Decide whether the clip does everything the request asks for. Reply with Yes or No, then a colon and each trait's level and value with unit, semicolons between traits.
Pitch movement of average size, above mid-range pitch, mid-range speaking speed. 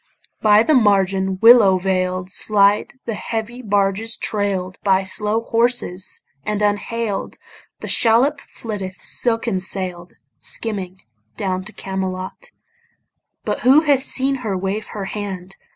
No: average, 3.2 semitones; high, 205 Hz; slow, 120 wpm